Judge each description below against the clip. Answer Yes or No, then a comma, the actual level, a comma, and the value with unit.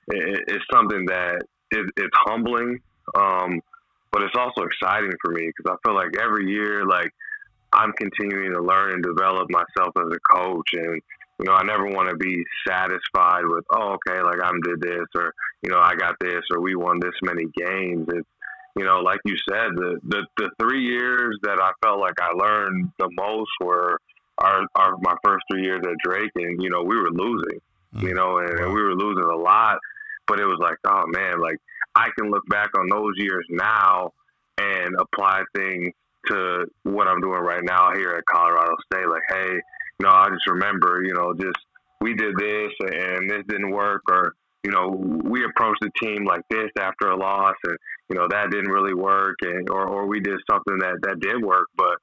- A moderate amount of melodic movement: Yes, average, 3.0 semitones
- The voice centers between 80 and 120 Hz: Yes, very low, 95 Hz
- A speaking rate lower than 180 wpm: No, fast, 205 wpm